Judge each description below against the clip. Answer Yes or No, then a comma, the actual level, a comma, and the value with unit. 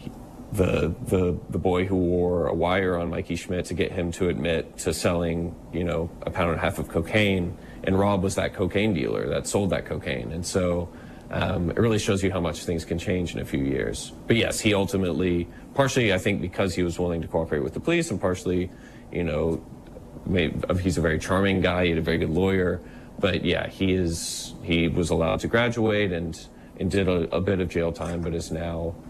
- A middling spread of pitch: No, narrow, 2.3 semitones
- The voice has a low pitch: Yes, very low, 90 Hz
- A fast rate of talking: Yes, fast, 220 wpm